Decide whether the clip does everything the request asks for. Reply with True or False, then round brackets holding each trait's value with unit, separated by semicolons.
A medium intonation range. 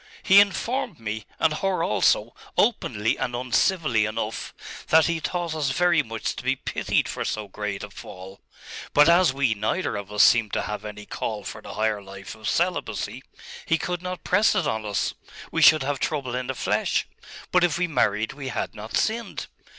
False (8.3 semitones)